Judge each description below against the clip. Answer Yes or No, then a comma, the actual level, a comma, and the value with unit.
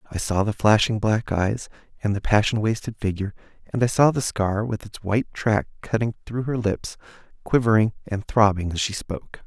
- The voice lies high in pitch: No, low, 105 Hz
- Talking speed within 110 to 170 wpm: No, average, 190 wpm